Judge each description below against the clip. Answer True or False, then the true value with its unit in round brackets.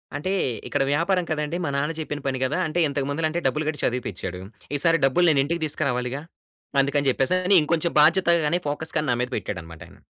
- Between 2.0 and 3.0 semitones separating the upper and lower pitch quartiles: False (3.5 semitones)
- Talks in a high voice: False (150 Hz)